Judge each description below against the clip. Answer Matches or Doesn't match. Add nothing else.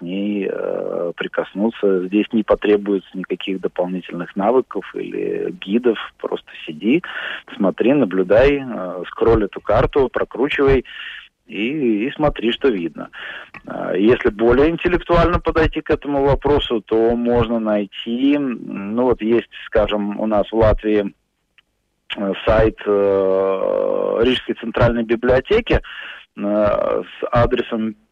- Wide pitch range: Matches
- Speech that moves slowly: Matches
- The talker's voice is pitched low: Matches